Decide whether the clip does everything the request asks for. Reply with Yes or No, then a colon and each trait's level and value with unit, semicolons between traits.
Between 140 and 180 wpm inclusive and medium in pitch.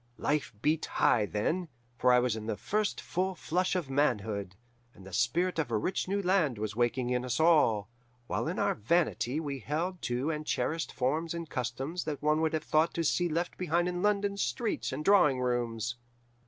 No: average, 195 wpm; medium, 150 Hz